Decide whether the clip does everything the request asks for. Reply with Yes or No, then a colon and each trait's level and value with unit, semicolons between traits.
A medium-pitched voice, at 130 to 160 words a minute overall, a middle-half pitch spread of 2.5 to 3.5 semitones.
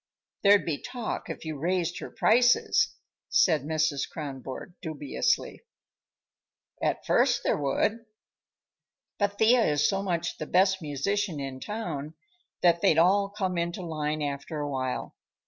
No: medium, 170 Hz; slow, 135 wpm; average, 5.2 semitones